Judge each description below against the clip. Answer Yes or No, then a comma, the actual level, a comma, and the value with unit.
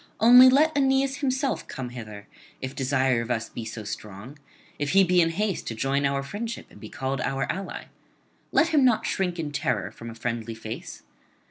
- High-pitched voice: No, medium, 140 Hz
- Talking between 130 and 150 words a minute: No, average, 195 wpm